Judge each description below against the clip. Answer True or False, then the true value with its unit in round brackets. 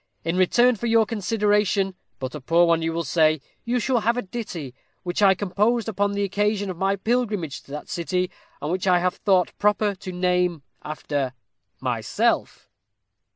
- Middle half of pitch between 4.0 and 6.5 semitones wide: False (3.6 semitones)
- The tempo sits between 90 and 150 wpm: False (175 wpm)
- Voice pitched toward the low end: False (190 Hz)